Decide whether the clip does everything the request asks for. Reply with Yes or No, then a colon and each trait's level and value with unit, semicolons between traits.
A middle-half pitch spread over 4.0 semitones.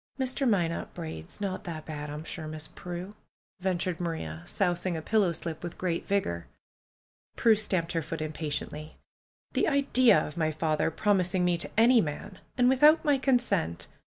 Yes: average, 5.0 semitones